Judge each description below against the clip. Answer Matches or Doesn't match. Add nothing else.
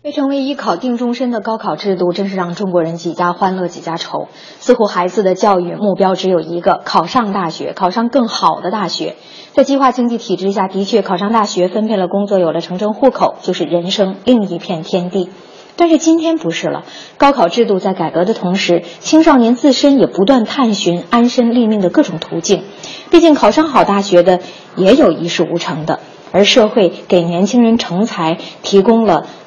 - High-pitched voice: Matches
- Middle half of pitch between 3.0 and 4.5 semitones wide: Doesn't match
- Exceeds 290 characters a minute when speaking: Matches